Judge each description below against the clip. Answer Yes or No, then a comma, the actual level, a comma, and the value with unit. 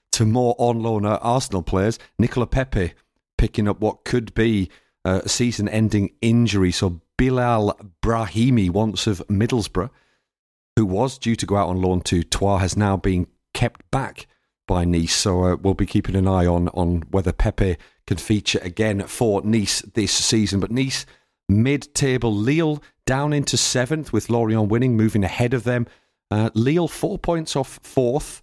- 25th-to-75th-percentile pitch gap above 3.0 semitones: Yes, average, 4.1 semitones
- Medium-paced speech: Yes, average, 170 wpm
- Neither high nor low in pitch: No, low, 110 Hz